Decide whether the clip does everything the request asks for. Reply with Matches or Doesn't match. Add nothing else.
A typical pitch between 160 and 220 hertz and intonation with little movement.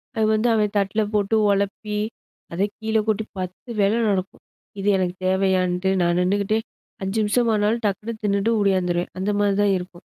Matches